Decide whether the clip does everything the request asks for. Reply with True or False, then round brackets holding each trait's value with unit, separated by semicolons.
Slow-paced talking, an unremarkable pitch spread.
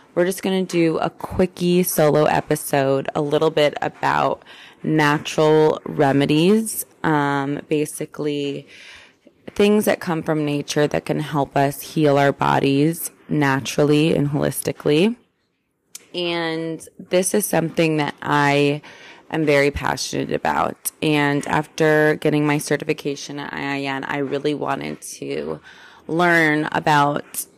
False (120 wpm; 2.2 semitones)